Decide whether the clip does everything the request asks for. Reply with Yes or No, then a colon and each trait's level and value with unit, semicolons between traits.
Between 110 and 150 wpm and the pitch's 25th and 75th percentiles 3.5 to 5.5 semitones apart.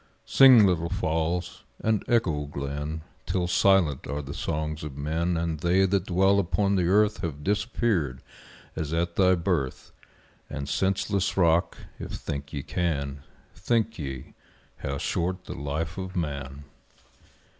Yes: average, 140 wpm; average, 4.6 semitones